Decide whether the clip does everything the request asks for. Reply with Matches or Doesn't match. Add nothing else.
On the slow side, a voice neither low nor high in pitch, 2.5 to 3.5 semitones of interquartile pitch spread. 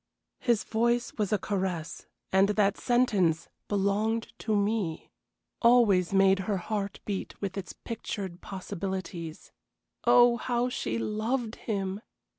Doesn't match